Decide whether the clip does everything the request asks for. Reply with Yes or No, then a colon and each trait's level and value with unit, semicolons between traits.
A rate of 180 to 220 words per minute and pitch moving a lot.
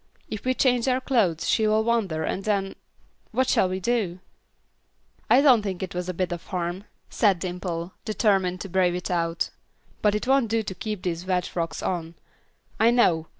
No: average, 190 wpm; average, 3.9 semitones